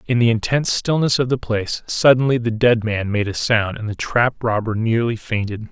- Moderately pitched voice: No, low, 115 Hz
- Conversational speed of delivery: No, fast, 210 wpm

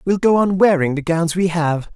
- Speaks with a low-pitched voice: No, medium, 170 Hz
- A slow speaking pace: No, fast, 245 wpm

